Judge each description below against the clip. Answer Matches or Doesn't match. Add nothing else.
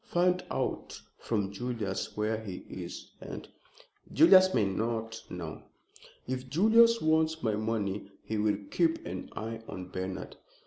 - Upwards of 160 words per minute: Doesn't match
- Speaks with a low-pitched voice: Matches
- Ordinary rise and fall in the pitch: Doesn't match